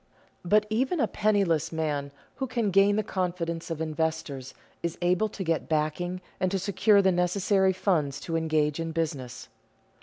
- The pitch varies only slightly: No, average, 3.7 semitones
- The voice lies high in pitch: No, medium, 175 Hz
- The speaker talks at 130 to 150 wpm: No, average, 160 wpm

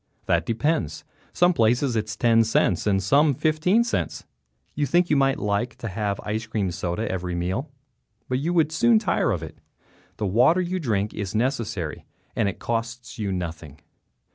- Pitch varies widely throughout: Yes, wide, 6.8 semitones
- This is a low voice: Yes, low, 115 Hz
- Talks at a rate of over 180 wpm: No, average, 175 wpm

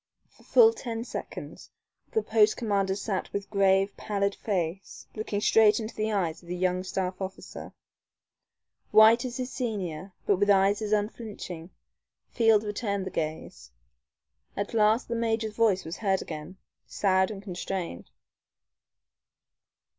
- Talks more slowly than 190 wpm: Yes, average, 140 wpm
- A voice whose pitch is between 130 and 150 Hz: No, high, 200 Hz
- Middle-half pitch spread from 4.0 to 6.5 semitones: No, average, 2.7 semitones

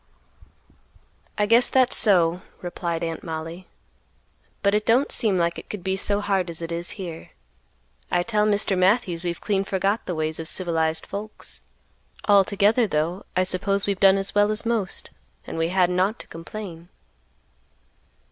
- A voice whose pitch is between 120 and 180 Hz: No, high, 190 Hz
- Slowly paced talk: No, average, 160 wpm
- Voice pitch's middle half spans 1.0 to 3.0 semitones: No, average, 3.4 semitones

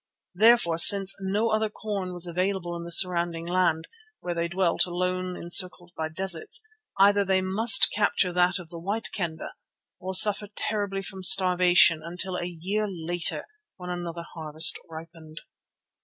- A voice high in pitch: No, medium, 180 Hz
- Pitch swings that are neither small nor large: No, narrow, 2.2 semitones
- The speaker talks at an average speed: Yes, average, 150 wpm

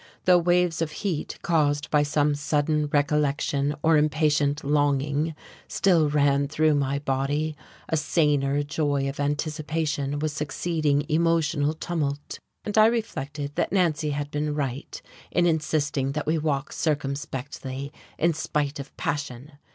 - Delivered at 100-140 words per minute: Yes, slow, 135 wpm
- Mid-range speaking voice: Yes, medium, 150 Hz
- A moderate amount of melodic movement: No, narrow, 1.7 semitones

